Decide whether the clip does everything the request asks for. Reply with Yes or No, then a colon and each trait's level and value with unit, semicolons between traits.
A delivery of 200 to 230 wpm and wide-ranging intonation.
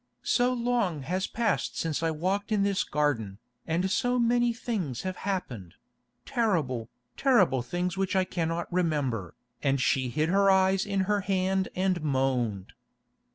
No: average, 145 wpm; wide, 6.5 semitones